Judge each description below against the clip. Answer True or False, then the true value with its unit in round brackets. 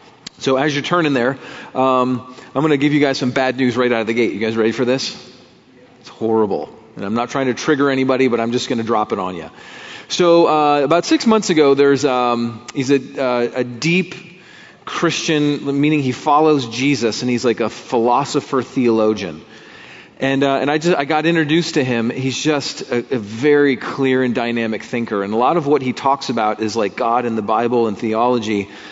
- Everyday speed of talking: False (210 wpm)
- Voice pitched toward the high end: False (130 Hz)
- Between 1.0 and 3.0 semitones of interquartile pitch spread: False (3.6 semitones)